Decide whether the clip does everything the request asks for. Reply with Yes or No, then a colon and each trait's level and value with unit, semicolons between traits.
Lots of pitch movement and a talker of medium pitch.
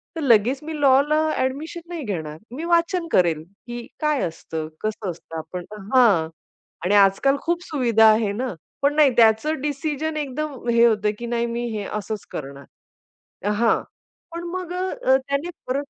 No: wide, 6.4 semitones; very high, 250 Hz